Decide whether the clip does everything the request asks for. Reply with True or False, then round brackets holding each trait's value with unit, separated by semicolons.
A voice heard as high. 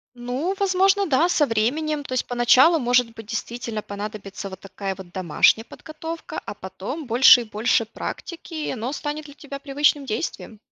True (250 Hz)